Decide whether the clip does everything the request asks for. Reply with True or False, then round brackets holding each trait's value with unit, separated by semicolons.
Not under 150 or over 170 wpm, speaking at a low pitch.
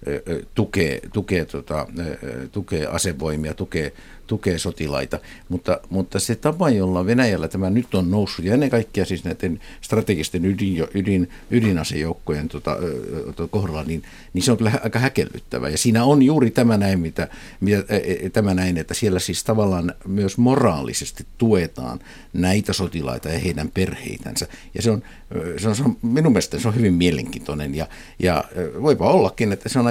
True (155 wpm; 95 Hz)